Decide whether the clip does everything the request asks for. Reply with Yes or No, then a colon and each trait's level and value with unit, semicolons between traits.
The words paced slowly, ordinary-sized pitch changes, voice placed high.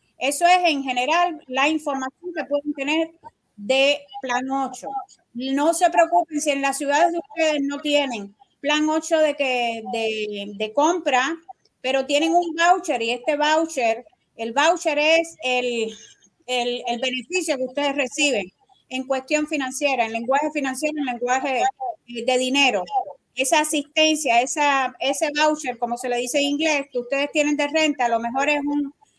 No: average, 160 wpm; average, 3.7 semitones; very high, 285 Hz